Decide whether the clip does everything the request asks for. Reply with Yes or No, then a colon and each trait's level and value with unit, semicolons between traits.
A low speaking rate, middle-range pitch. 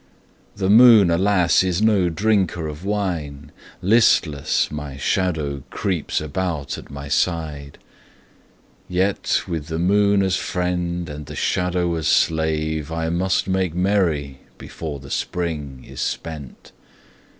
No: slow, 125 wpm; very low, 85 Hz